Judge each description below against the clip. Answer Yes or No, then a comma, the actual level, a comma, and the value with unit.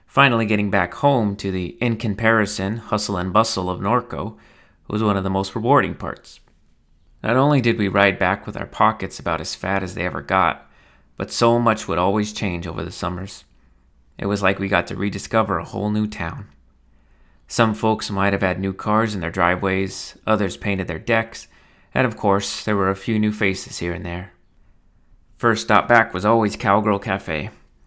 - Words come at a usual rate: Yes, average, 190 wpm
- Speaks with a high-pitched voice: No, low, 100 Hz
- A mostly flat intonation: No, average, 3.4 semitones